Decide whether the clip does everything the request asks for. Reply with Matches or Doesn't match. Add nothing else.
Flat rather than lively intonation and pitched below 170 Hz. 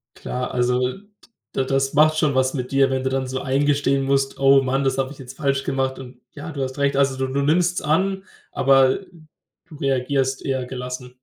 Matches